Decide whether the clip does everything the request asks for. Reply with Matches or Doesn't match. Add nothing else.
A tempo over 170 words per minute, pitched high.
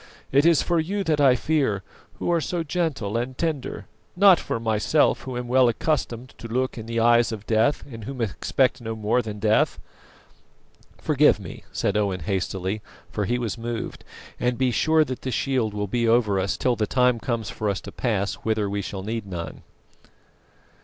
Doesn't match